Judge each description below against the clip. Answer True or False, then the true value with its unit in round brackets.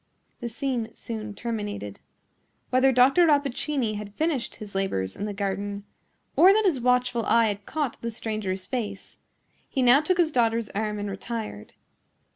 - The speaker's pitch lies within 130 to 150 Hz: False (230 Hz)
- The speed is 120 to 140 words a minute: False (155 wpm)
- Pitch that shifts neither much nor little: True (4.3 semitones)